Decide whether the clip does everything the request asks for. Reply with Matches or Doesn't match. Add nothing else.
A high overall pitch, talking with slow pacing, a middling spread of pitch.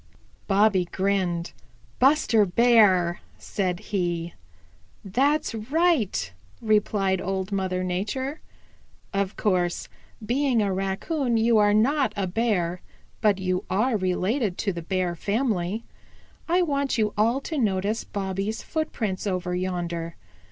Matches